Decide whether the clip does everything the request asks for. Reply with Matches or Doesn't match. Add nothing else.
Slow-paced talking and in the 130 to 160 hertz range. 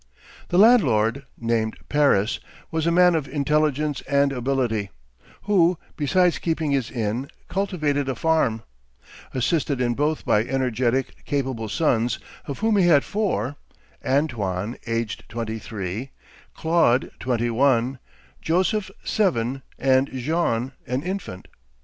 Matches